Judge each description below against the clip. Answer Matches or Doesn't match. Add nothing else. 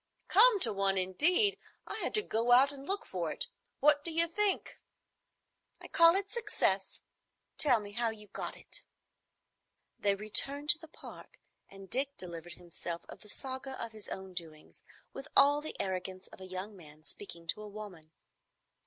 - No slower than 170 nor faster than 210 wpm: Matches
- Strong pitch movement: Matches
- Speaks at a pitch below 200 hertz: Doesn't match